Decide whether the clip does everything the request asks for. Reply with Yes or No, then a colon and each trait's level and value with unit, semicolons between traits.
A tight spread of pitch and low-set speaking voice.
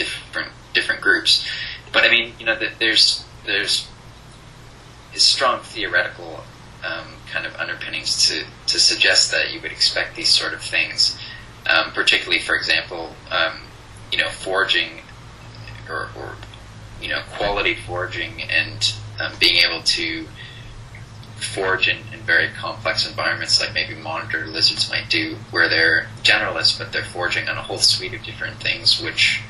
Yes: narrow, 1.0 semitones; low, 110 Hz